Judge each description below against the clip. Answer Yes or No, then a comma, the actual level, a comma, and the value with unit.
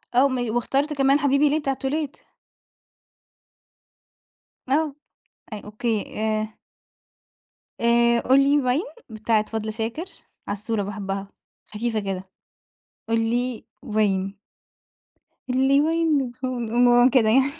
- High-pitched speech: Yes, high, 240 Hz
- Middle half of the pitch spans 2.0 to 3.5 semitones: No, average, 4.1 semitones